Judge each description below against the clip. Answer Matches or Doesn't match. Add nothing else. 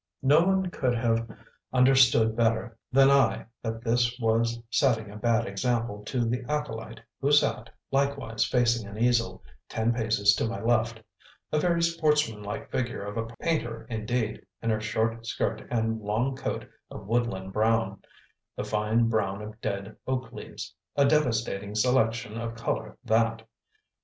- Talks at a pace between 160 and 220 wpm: Doesn't match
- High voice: Doesn't match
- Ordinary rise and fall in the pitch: Doesn't match